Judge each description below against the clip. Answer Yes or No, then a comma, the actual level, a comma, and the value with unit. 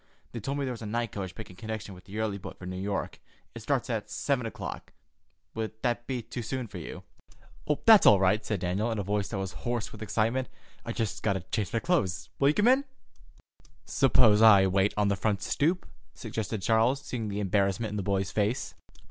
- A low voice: Yes, low, 110 Hz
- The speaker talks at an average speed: No, fast, 215 wpm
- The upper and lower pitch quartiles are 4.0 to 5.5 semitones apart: No, average, 3.3 semitones